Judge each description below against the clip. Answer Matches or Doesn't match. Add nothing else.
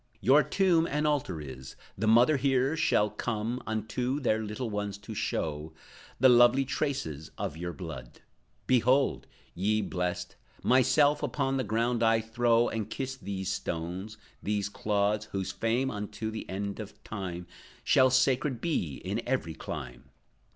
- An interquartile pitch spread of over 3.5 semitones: Matches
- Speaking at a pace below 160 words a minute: Matches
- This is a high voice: Doesn't match